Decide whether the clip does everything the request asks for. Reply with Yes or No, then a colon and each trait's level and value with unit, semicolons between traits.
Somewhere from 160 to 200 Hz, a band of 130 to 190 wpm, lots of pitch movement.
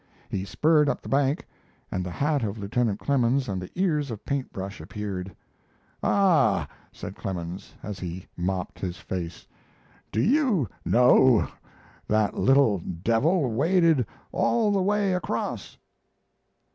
No: low, 120 Hz; slow, 135 wpm; wide, 7.7 semitones